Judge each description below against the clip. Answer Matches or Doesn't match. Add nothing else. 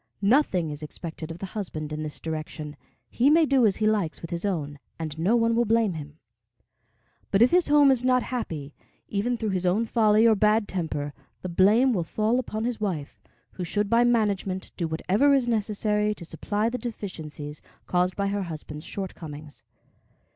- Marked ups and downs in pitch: Matches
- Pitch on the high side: Matches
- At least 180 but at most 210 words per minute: Matches